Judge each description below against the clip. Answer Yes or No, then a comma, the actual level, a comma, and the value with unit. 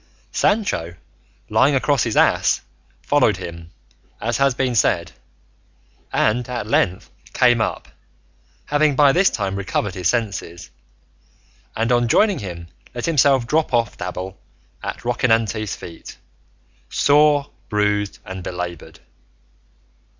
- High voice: No, low, 115 Hz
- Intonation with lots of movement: Yes, wide, 6.3 semitones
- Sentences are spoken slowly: Yes, slow, 115 wpm